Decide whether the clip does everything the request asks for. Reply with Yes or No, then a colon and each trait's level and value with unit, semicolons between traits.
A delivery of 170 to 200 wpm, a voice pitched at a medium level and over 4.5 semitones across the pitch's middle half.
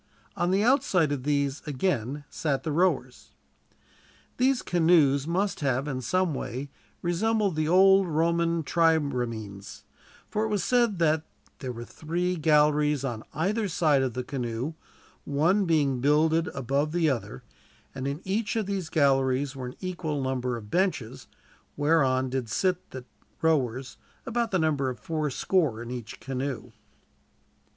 No: average, 145 wpm; medium, 150 Hz; average, 5.1 semitones